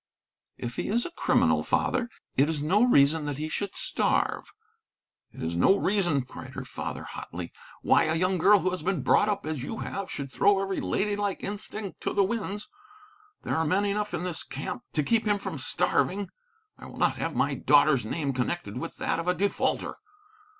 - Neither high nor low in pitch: Yes, medium, 180 Hz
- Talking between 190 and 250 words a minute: Yes, average, 200 wpm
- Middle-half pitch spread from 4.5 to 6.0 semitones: Yes, wide, 5.6 semitones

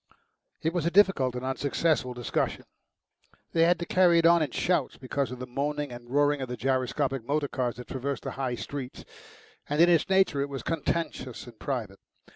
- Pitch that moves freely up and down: No, average, 4.5 semitones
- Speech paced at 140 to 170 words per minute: No, average, 195 wpm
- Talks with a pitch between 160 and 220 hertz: No, medium, 140 Hz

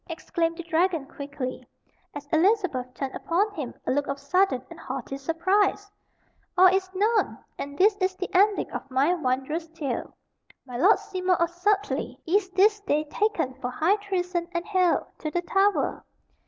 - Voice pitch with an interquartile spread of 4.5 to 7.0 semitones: Yes, average, 5.2 semitones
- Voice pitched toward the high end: Yes, very high, 345 Hz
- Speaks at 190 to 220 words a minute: No, average, 165 wpm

